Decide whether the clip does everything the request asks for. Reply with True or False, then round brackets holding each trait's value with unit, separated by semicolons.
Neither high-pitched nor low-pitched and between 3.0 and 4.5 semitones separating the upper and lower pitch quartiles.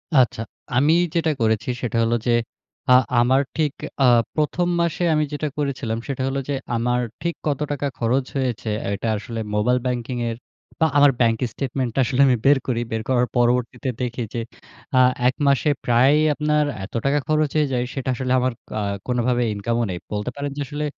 False (130 Hz; 3.4 semitones)